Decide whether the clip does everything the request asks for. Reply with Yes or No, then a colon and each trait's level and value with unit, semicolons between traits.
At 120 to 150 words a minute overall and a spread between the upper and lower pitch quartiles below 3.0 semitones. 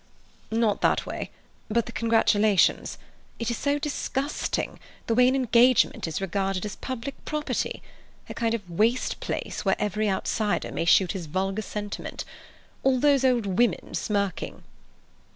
No: slow, 135 wpm; average, 4.1 semitones